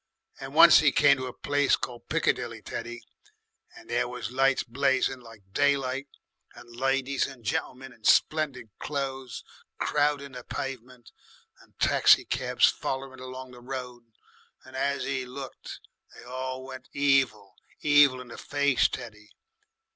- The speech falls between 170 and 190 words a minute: No, average, 140 wpm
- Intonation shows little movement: Yes, narrow, 2.0 semitones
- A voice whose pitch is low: Yes, low, 130 Hz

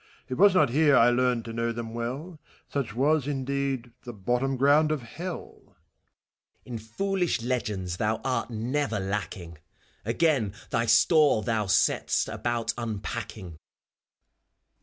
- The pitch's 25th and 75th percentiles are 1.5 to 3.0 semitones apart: No, average, 4.0 semitones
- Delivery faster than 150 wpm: No, average, 140 wpm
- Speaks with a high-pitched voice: No, low, 120 Hz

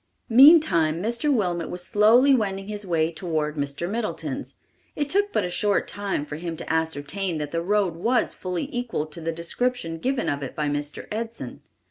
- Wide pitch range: Yes, wide, 6.0 semitones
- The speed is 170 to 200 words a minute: Yes, average, 180 wpm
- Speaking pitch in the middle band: Yes, medium, 180 Hz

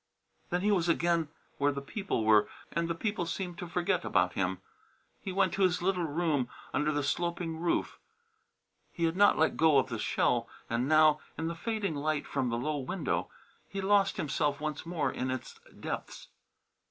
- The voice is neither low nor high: Yes, medium, 165 Hz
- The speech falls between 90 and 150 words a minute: No, average, 190 wpm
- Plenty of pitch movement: No, average, 3.8 semitones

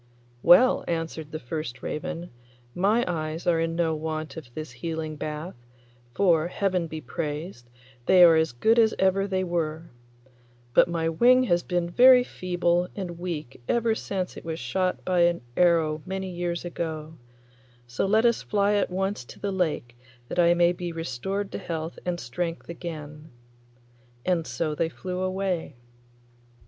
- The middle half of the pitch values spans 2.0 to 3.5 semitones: Yes, average, 2.8 semitones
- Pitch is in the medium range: Yes, medium, 170 Hz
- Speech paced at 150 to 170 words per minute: Yes, average, 160 wpm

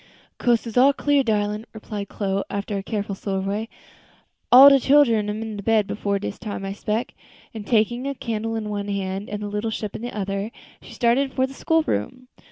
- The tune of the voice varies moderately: Yes, average, 3.1 semitones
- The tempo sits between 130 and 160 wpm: No, average, 195 wpm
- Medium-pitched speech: No, high, 215 Hz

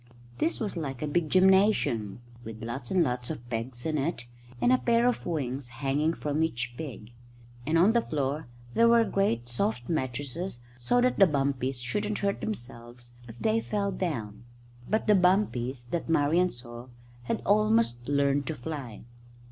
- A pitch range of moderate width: No, wide, 7.9 semitones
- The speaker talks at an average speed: Yes, average, 165 wpm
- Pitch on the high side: No, medium, 145 Hz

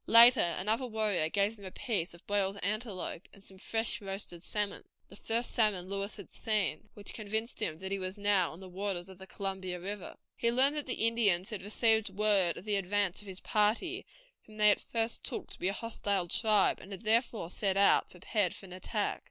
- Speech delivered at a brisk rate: Yes, fast, 210 wpm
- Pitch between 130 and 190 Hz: No, high, 205 Hz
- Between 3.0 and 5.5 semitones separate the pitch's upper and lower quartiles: No, narrow, 2.5 semitones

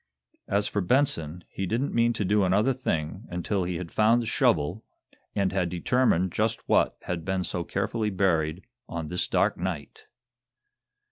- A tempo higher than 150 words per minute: Yes, average, 160 wpm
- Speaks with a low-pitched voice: Yes, very low, 95 Hz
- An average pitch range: Yes, average, 3.8 semitones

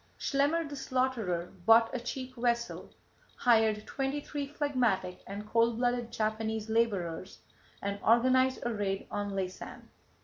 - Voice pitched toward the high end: Yes, high, 230 Hz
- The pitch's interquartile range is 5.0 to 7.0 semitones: No, average, 3.9 semitones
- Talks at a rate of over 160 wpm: No, slow, 135 wpm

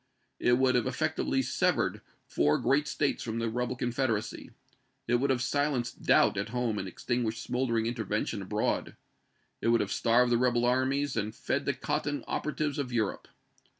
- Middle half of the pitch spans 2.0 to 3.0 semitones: Yes, narrow, 2.4 semitones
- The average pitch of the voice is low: Yes, low, 125 Hz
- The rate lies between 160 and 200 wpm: Yes, average, 165 wpm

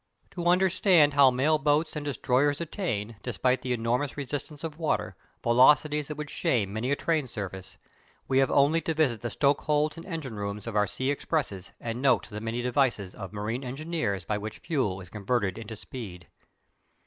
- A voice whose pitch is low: Yes, low, 130 Hz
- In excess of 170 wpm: Yes, average, 180 wpm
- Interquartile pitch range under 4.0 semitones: No, wide, 5.6 semitones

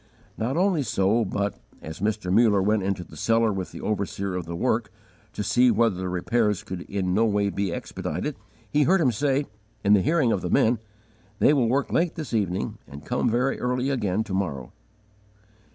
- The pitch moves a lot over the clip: No, average, 4.7 semitones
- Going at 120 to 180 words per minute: No, average, 200 wpm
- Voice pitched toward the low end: Yes, low, 105 Hz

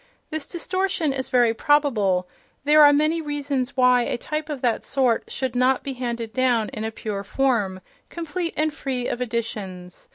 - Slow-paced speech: No, average, 170 wpm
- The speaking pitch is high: Yes, very high, 255 Hz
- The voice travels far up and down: No, average, 4.3 semitones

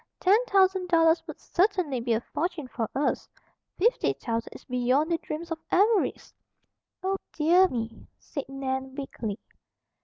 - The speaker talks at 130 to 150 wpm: Yes, average, 145 wpm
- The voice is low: No, very high, 305 Hz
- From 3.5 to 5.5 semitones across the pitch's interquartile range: No, wide, 6.0 semitones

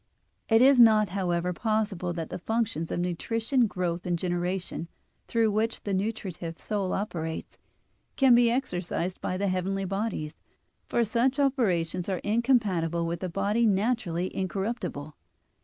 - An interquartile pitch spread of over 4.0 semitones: Yes, average, 4.5 semitones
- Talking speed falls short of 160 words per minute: Yes, average, 140 wpm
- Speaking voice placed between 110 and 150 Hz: No, high, 195 Hz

